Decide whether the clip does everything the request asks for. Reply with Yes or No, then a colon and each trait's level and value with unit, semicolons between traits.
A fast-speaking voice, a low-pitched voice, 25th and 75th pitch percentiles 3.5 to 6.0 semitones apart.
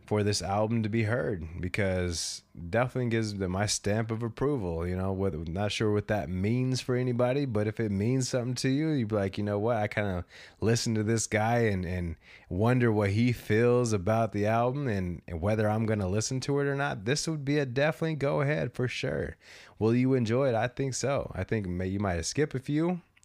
Yes: fast, 225 wpm; low, 110 Hz; average, 3.9 semitones